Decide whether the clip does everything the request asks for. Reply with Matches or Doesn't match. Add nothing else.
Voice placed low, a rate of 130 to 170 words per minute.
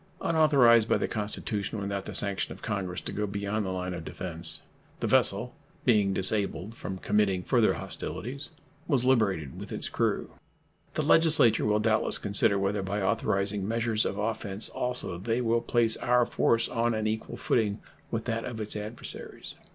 Matches